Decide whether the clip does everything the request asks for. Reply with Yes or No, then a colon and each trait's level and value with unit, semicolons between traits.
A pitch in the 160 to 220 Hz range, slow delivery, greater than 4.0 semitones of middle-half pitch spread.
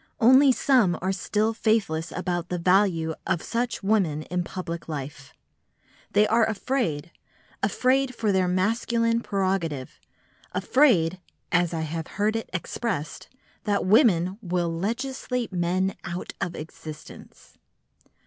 Yes: high, 190 Hz; slow, 120 wpm; average, 5.0 semitones